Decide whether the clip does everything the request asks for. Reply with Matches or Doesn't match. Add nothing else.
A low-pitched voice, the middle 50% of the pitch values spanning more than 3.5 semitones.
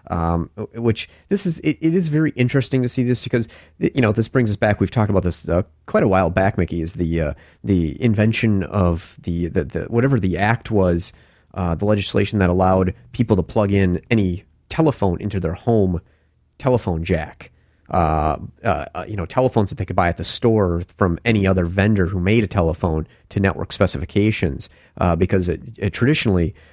Matches